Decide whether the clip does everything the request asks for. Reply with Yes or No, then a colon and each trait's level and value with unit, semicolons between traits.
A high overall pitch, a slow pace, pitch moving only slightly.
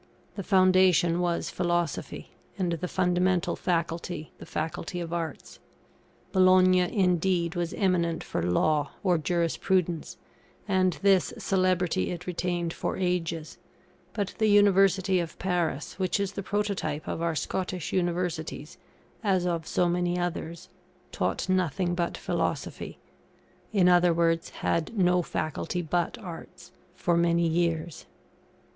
No: medium, 175 Hz; slow, 125 wpm; narrow, 1.7 semitones